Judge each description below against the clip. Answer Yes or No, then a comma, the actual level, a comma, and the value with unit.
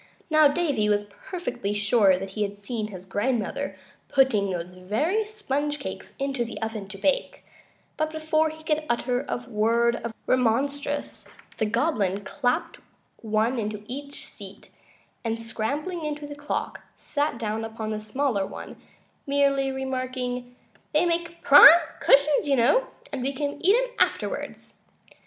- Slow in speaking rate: No, average, 145 wpm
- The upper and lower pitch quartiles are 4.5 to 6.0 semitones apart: Yes, wide, 5.4 semitones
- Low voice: No, very high, 255 Hz